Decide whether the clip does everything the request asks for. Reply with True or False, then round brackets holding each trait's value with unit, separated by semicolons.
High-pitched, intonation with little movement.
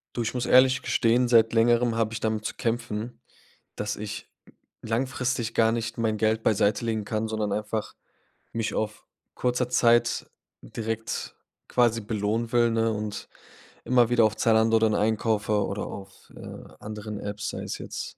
False (115 Hz; 1.6 semitones)